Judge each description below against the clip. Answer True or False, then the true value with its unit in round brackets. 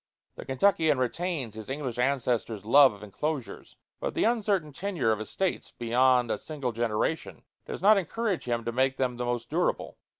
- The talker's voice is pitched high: False (130 Hz)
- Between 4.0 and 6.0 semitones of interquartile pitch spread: True (5.3 semitones)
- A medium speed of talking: True (170 wpm)